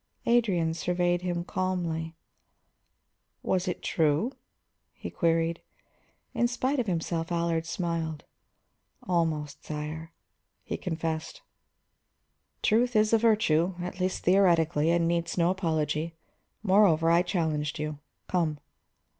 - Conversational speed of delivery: No, slow, 110 wpm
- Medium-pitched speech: Yes, medium, 170 Hz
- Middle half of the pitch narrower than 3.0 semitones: Yes, narrow, 2.4 semitones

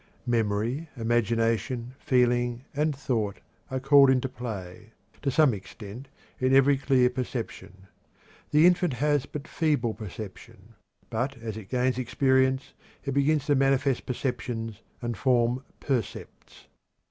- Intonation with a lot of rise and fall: No, average, 3.1 semitones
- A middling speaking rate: No, slow, 125 wpm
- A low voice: Yes, low, 125 Hz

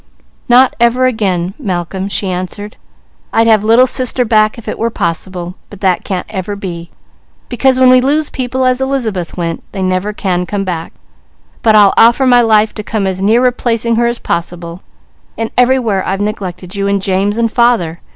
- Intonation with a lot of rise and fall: No, average, 4.3 semitones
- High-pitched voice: Yes, high, 210 Hz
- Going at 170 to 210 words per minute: Yes, average, 180 wpm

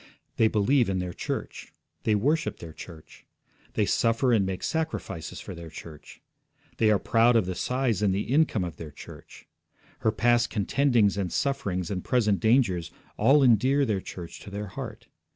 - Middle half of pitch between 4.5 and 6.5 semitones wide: Yes, average, 5.2 semitones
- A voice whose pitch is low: Yes, low, 105 Hz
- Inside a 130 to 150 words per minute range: No, average, 170 wpm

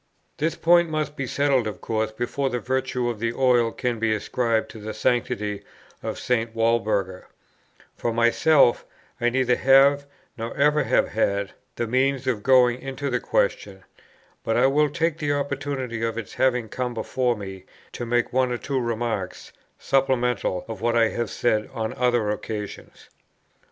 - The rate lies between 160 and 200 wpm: Yes, average, 165 wpm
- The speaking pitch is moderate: No, low, 120 Hz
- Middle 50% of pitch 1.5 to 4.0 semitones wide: Yes, average, 2.9 semitones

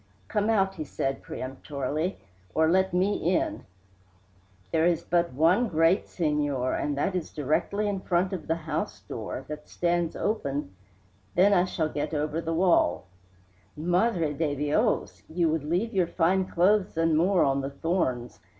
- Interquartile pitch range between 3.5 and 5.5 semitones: Yes, average, 4.1 semitones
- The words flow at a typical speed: Yes, average, 165 wpm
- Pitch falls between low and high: Yes, medium, 165 Hz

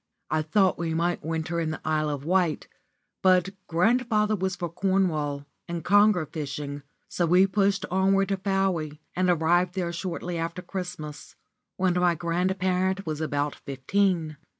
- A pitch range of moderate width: Yes, average, 3.2 semitones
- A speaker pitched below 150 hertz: No, medium, 175 Hz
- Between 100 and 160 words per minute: Yes, average, 150 wpm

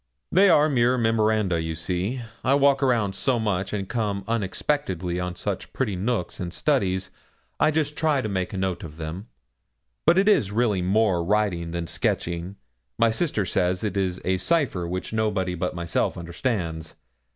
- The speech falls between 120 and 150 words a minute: No, average, 165 wpm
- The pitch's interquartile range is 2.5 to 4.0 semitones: No, average, 4.9 semitones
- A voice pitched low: Yes, low, 100 Hz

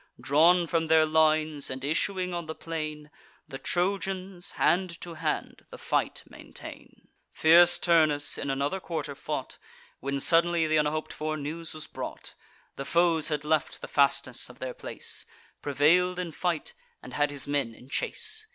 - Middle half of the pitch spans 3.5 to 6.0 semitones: No, average, 3.0 semitones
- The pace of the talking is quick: No, average, 160 wpm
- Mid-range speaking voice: Yes, medium, 155 Hz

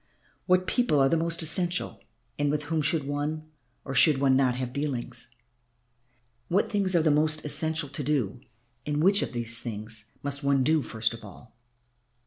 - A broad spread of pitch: No, average, 3.8 semitones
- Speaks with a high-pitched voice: No, medium, 145 Hz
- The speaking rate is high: No, average, 175 wpm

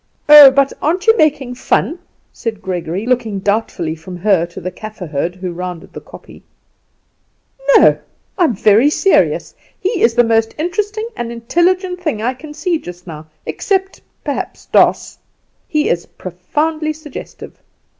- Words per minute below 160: Yes, average, 150 wpm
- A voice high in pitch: Yes, high, 240 Hz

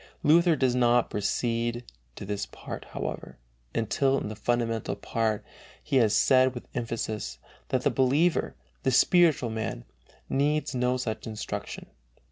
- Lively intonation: No, average, 3.2 semitones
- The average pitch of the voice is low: Yes, low, 120 Hz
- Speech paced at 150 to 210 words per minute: No, average, 140 wpm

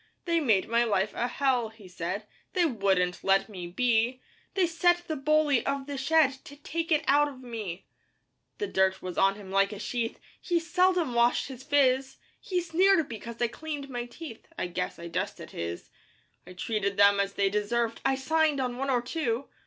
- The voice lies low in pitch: No, high, 245 Hz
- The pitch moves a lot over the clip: Yes, wide, 6.8 semitones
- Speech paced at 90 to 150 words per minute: No, average, 190 wpm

